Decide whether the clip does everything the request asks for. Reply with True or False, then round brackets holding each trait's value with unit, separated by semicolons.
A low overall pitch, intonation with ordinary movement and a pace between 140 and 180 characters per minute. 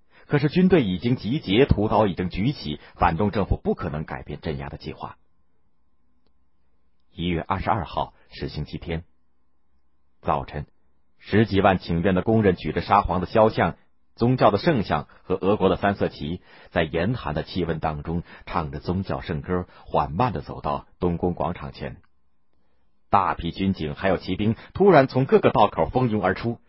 False (85 Hz; 4.4 semitones; 245 characters per minute)